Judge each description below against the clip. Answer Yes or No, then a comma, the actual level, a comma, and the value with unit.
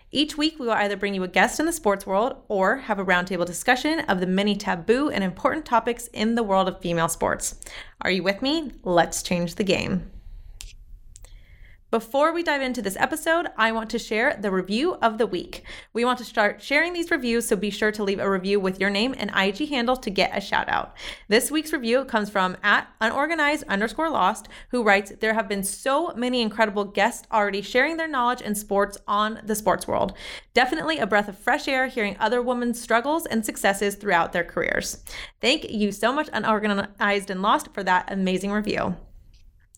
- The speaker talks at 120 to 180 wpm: No, average, 200 wpm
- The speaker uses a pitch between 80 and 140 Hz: No, high, 215 Hz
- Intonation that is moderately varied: Yes, average, 4.3 semitones